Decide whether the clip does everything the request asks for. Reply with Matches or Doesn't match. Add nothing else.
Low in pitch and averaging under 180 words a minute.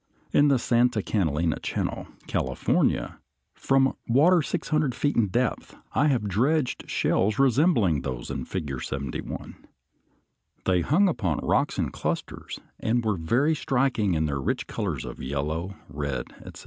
Matches